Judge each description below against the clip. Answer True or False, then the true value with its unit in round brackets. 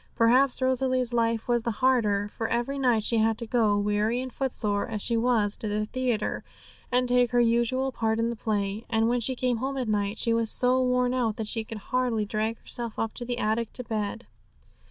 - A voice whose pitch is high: True (230 Hz)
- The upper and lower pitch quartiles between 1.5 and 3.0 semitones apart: True (2.4 semitones)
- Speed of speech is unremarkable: False (215 wpm)